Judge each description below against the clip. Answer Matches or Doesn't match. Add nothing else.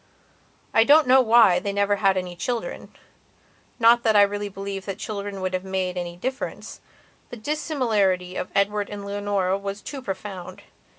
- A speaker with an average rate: Matches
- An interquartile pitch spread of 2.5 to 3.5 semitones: Matches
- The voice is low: Doesn't match